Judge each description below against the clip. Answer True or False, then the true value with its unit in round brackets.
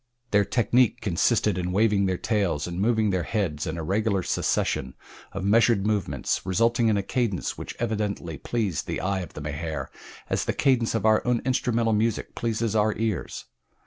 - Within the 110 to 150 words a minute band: False (175 wpm)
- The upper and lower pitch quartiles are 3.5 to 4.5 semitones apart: True (3.8 semitones)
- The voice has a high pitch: False (105 Hz)